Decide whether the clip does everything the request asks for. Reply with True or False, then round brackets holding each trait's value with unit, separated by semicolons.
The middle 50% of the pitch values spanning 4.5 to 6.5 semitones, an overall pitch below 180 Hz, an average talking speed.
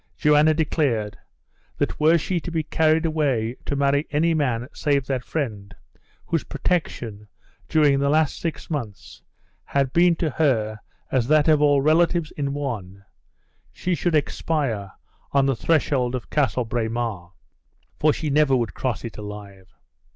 True (5.1 semitones; 140 Hz; 150 wpm)